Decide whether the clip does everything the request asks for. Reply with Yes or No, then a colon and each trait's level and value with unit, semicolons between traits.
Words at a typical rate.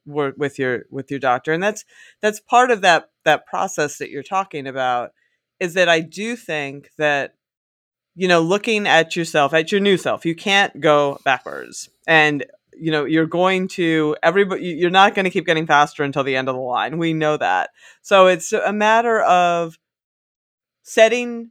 Yes: average, 185 wpm